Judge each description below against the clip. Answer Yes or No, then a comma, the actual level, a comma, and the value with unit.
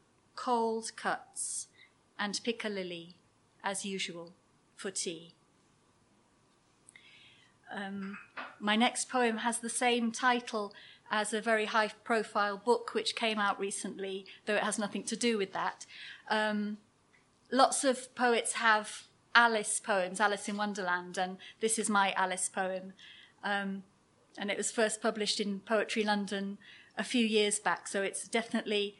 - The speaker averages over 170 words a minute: No, average, 140 wpm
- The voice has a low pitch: No, high, 210 Hz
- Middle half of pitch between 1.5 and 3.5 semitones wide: Yes, narrow, 2.5 semitones